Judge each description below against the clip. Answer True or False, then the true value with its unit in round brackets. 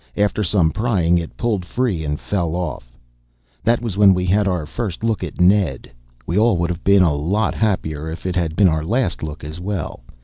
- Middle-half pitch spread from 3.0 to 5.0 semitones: True (4.4 semitones)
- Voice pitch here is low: True (90 Hz)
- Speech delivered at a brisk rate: True (210 wpm)